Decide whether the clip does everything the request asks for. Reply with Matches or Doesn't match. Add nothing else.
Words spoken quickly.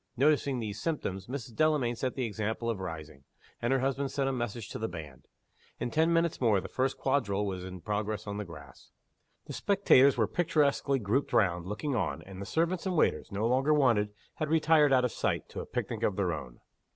Matches